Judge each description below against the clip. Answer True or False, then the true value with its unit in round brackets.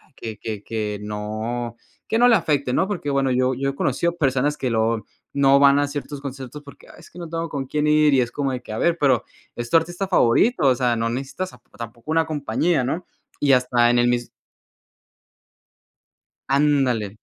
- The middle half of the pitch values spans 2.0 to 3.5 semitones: False (3.9 semitones)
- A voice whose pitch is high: False (135 Hz)